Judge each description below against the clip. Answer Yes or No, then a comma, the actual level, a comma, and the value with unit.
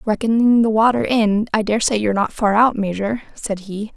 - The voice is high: Yes, high, 215 Hz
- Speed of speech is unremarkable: Yes, average, 195 wpm